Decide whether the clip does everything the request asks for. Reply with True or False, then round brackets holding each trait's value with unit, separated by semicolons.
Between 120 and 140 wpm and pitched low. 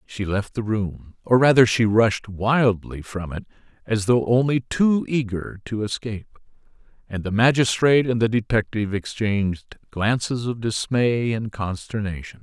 True (135 wpm; 110 Hz)